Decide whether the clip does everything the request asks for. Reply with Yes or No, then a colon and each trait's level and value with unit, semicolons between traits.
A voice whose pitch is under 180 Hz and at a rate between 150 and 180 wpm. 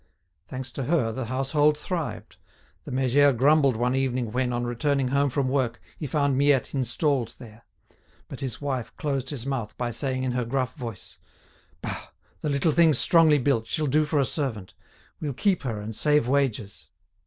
Yes: low, 135 Hz; average, 175 wpm